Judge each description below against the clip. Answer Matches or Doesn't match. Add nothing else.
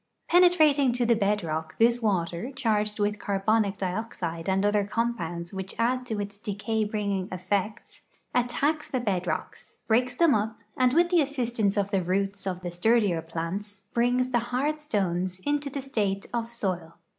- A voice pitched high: Matches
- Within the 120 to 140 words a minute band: Doesn't match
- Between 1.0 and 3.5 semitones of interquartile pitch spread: Doesn't match